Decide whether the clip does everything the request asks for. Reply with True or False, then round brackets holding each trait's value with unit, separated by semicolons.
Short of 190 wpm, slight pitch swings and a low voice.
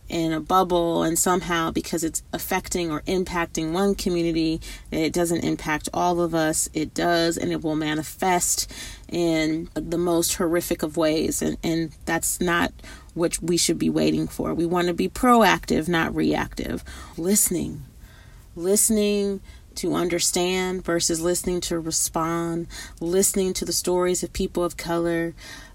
False (145 wpm; 2.1 semitones; 170 Hz)